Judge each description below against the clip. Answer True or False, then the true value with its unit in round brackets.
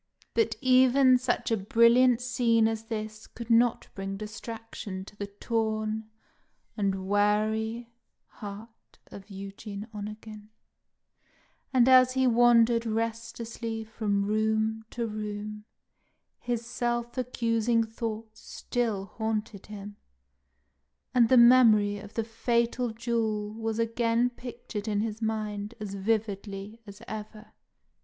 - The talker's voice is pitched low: False (220 Hz)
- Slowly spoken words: True (115 wpm)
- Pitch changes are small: True (1.9 semitones)